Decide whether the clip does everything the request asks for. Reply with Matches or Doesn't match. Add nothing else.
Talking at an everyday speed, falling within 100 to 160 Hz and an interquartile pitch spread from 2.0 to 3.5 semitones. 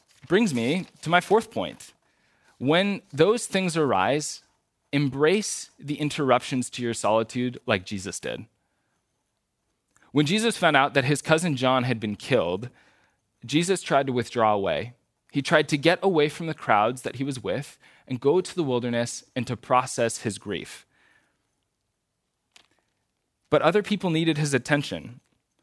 Doesn't match